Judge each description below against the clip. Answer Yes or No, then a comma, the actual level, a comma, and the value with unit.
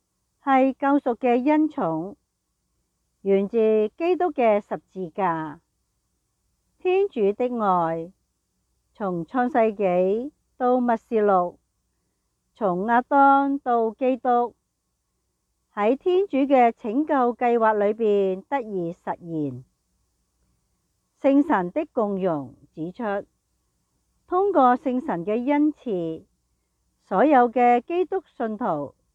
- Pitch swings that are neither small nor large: No, wide, 6.2 semitones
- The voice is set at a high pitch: Yes, high, 230 Hz